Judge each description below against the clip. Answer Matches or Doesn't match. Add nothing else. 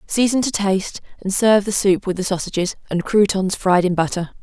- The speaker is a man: Doesn't match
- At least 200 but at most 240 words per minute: Matches